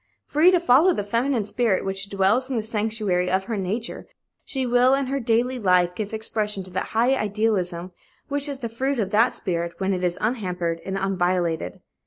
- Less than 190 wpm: No, average, 195 wpm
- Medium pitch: No, high, 215 Hz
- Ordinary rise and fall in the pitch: Yes, average, 4.9 semitones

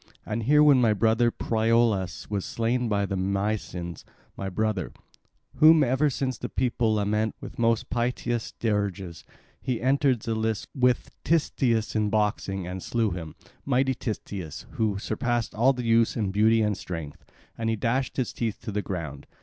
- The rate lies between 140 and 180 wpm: Yes, average, 160 wpm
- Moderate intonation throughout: Yes, average, 3.2 semitones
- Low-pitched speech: Yes, low, 110 Hz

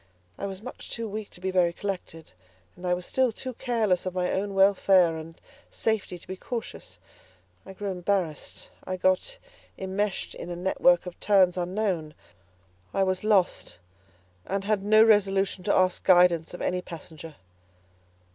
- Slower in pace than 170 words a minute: Yes, average, 160 wpm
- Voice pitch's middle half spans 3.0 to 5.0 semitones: No, narrow, 2.4 semitones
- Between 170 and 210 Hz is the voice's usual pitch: Yes, high, 190 Hz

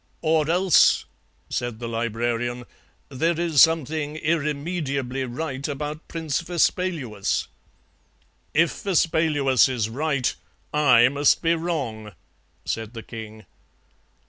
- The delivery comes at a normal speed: No, slow, 100 wpm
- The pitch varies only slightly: No, average, 5.0 semitones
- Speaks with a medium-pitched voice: Yes, medium, 145 Hz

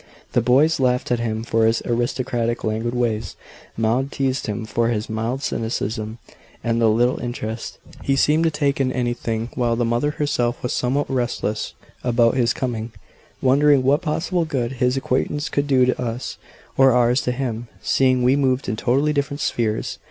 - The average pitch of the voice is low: Yes, low, 125 Hz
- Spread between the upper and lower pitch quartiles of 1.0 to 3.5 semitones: Yes, narrow, 2.6 semitones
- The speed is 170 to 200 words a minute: Yes, average, 175 wpm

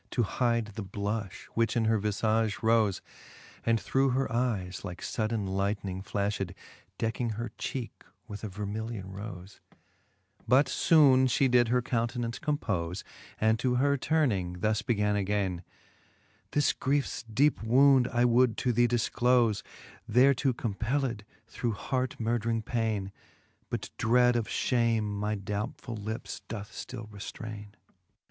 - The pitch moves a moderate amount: Yes, average, 3.0 semitones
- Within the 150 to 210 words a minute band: No, slow, 135 wpm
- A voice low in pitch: Yes, low, 115 Hz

